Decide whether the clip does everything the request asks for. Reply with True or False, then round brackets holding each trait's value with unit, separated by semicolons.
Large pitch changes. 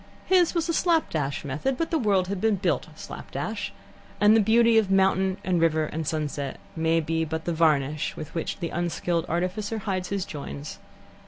False (5.0 semitones)